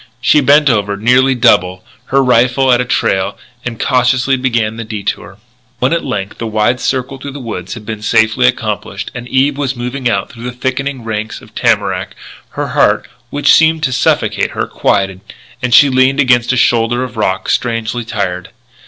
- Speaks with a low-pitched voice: Yes, low, 125 Hz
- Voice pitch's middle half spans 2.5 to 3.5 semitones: Yes, average, 3.1 semitones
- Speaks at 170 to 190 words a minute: Yes, average, 180 wpm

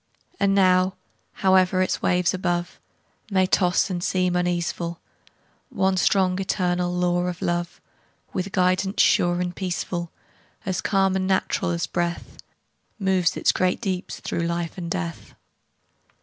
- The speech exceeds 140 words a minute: No, slow, 135 wpm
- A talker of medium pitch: Yes, medium, 180 Hz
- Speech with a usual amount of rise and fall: No, narrow, 1.3 semitones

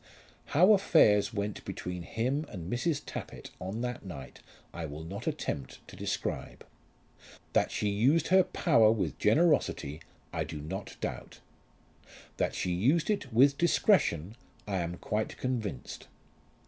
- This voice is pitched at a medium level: No, low, 110 Hz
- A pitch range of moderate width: No, wide, 7.9 semitones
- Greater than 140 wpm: No, slow, 135 wpm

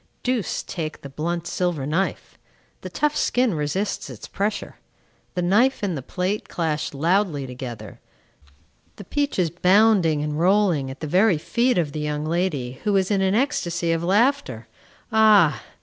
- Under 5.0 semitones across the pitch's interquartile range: No, average, 5.3 semitones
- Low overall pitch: No, medium, 175 Hz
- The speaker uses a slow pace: No, average, 155 wpm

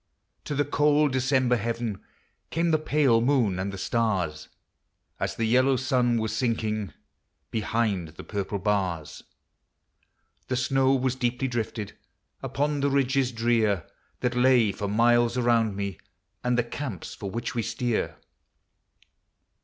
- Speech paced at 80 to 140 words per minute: Yes, slow, 135 wpm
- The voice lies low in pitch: Yes, low, 120 Hz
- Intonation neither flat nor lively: Yes, average, 3.5 semitones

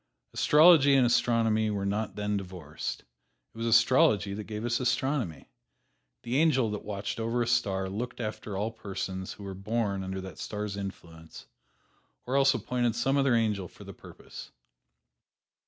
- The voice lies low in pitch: Yes, low, 110 Hz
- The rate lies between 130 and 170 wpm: Yes, average, 155 wpm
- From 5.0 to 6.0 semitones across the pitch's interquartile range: No, average, 3.6 semitones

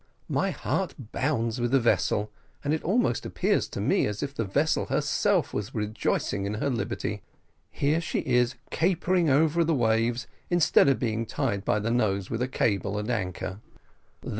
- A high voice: No, low, 120 Hz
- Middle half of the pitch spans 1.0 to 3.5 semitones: No, average, 5.3 semitones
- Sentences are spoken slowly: No, average, 170 wpm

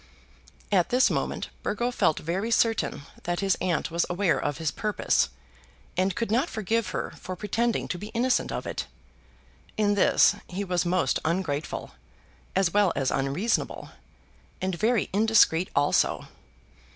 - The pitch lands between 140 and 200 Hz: Yes, high, 190 Hz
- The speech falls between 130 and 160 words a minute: Yes, average, 145 wpm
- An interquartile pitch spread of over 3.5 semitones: Yes, average, 4.4 semitones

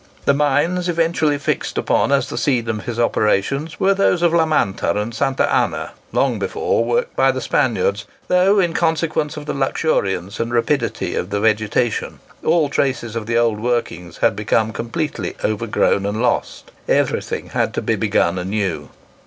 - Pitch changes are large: Yes, wide, 7.0 semitones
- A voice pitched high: No, low, 125 Hz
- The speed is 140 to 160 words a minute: No, average, 170 wpm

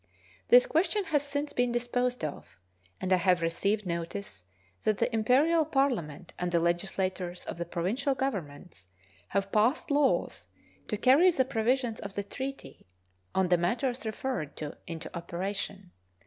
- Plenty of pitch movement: Yes, wide, 7.1 semitones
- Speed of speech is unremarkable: Yes, average, 150 wpm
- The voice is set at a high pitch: Yes, high, 210 Hz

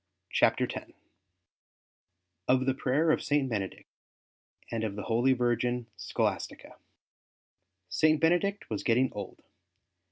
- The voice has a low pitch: Yes, low, 125 Hz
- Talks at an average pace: No, slow, 115 wpm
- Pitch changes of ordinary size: Yes, average, 4.4 semitones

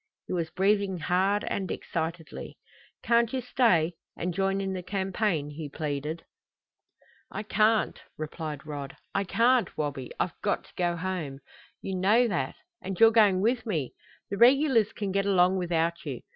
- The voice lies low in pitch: No, medium, 185 Hz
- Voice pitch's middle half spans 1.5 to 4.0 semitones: No, average, 4.4 semitones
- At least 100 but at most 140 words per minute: No, average, 160 wpm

